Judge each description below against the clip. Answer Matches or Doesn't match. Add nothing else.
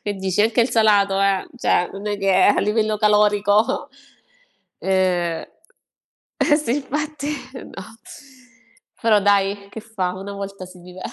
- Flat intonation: Matches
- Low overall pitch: Doesn't match